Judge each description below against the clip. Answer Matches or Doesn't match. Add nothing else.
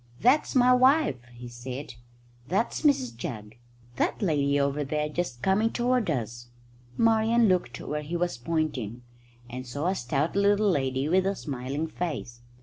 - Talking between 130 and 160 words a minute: Matches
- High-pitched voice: Doesn't match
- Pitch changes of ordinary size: Doesn't match